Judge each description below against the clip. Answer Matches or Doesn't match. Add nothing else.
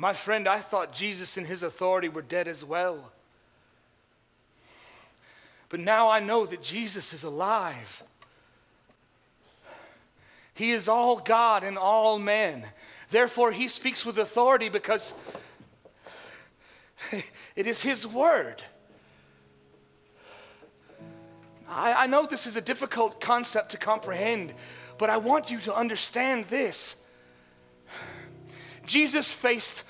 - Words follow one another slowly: Matches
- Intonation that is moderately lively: Matches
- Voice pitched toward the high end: Matches